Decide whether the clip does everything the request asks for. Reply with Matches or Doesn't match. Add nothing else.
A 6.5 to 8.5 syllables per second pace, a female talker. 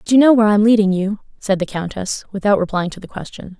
Matches